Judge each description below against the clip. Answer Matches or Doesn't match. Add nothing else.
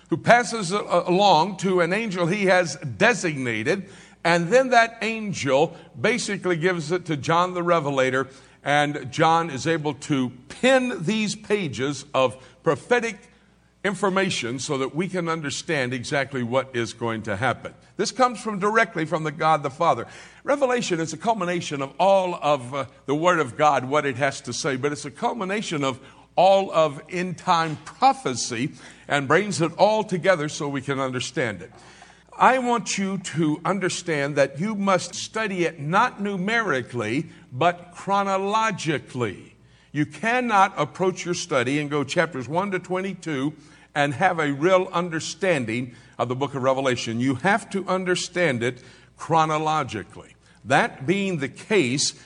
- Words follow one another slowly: Doesn't match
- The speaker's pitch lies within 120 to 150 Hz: Doesn't match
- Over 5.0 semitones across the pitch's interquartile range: Matches